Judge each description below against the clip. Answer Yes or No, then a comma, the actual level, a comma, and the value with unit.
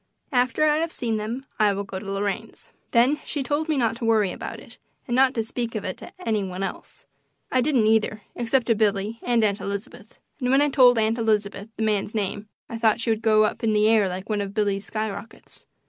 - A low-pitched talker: No, high, 220 Hz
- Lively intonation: No, average, 3.0 semitones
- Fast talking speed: Yes, fast, 230 wpm